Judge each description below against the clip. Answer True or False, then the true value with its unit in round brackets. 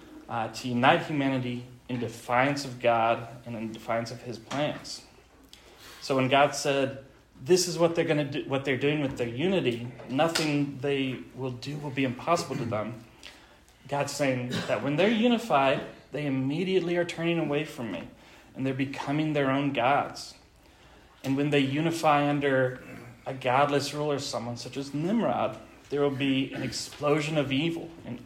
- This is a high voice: False (135 Hz)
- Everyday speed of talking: True (170 wpm)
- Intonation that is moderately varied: True (3.0 semitones)